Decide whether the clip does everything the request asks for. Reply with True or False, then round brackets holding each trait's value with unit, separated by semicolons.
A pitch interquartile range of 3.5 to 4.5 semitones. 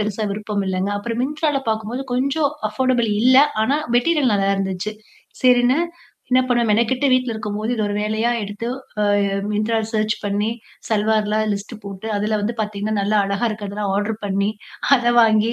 False (2.7 semitones)